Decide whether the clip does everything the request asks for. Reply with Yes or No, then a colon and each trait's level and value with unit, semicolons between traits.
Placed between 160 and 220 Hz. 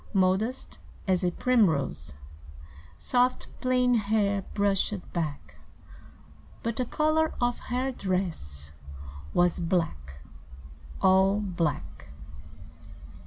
Yes: high, 190 Hz